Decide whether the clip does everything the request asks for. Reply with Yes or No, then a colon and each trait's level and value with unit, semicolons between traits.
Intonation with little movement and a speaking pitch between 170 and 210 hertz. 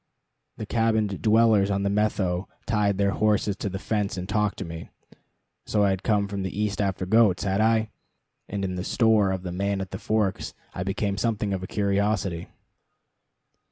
No: narrow, 1.9 semitones; low, 100 Hz